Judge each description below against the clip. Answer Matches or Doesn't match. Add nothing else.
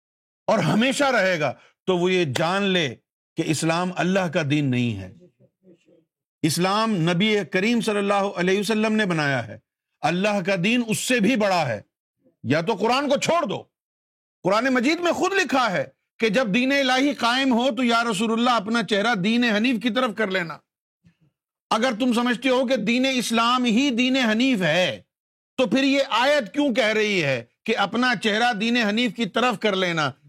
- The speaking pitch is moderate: Doesn't match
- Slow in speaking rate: Doesn't match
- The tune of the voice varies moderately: Doesn't match